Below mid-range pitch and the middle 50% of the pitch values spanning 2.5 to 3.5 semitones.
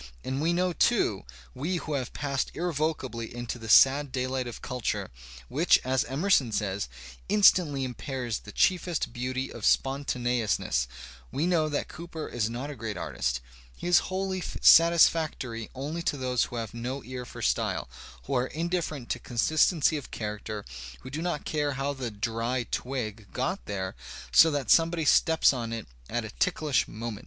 No: low, 130 Hz; average, 5.1 semitones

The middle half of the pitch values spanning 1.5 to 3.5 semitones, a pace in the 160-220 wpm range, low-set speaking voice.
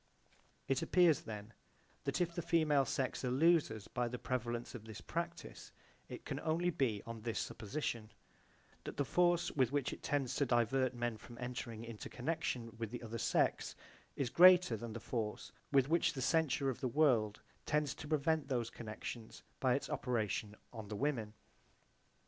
No: average, 4.5 semitones; average, 170 wpm; low, 125 Hz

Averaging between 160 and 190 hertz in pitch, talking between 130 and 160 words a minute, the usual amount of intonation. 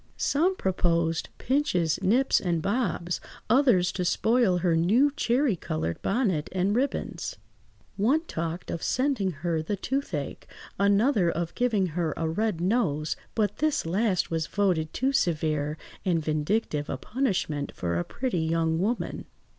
No: medium, 185 Hz; average, 140 wpm; wide, 6.5 semitones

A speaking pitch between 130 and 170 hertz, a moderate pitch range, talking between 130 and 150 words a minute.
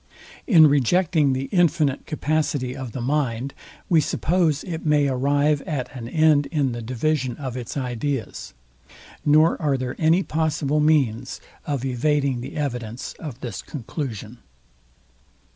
Yes: medium, 140 Hz; average, 3.4 semitones; slow, 135 wpm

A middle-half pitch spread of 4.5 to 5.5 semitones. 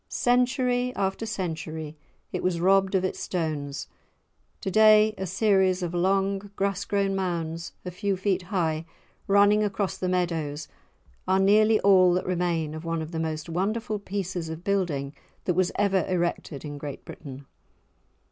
No: average, 3.3 semitones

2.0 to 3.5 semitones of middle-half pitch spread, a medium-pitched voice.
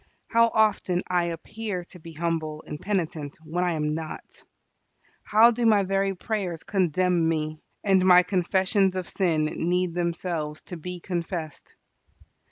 Yes: average, 2.8 semitones; medium, 180 Hz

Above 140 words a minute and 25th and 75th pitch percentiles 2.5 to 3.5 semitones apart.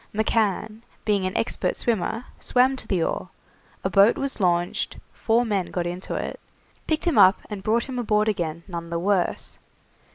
No: average, 170 wpm; average, 4.2 semitones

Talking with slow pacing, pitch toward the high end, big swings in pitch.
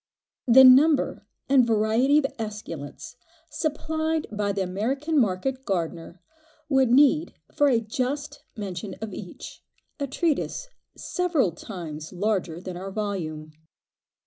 Yes: slow, 120 wpm; high, 220 Hz; wide, 7.0 semitones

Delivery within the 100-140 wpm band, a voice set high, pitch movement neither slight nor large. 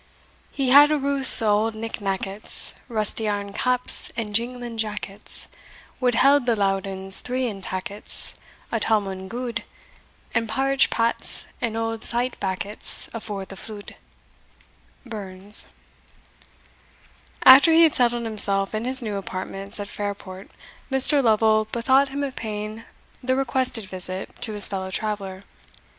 Yes: slow, 135 wpm; high, 220 Hz; average, 3.7 semitones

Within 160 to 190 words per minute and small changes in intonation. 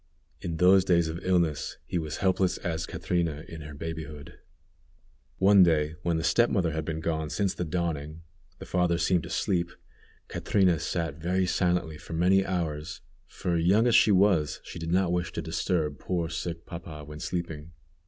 Yes: average, 175 wpm; narrow, 2.3 semitones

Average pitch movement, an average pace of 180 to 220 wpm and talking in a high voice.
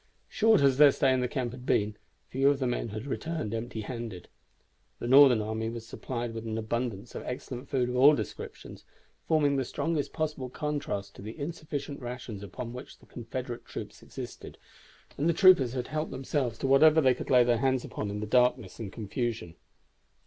No: average, 3.7 semitones; average, 190 wpm; low, 125 Hz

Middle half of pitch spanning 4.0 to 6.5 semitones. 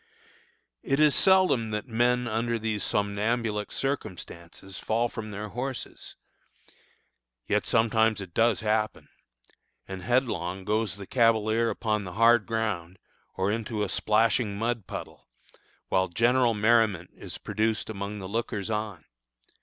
No: narrow, 2.4 semitones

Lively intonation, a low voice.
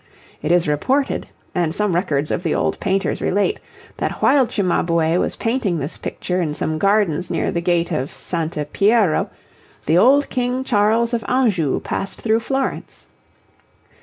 No: wide, 5.8 semitones; high, 195 Hz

